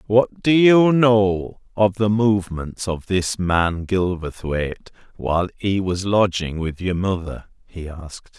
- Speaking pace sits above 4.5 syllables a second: No, 3.8 syllables/s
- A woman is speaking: No, male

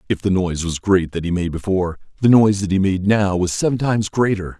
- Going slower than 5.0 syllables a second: No, 6.2 syllables/s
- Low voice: Yes, very low, 95 Hz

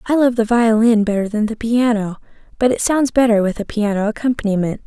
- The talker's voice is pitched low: No, high, 225 Hz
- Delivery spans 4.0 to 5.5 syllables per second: No, 5.7 syllables/s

